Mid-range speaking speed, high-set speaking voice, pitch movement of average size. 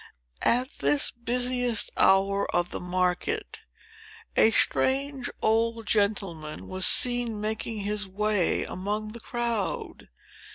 No: slow, 110 wpm; high, 215 Hz; average, 3.7 semitones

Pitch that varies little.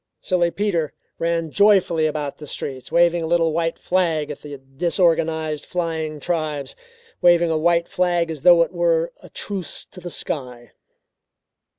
Yes: narrow, 2.0 semitones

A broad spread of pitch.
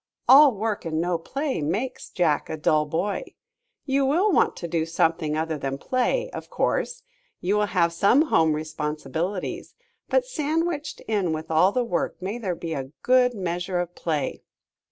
Yes: wide, 8.1 semitones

